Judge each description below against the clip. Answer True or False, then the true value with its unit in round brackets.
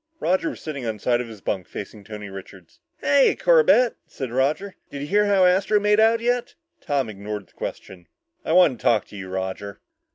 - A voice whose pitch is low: True (130 Hz)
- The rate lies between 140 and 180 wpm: False (205 wpm)